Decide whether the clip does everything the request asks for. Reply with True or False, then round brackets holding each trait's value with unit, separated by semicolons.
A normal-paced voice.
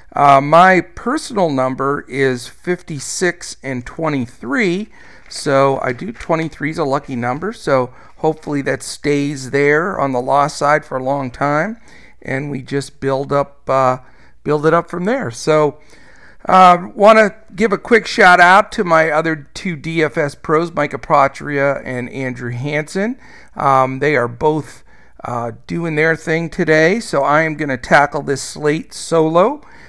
True (160 wpm)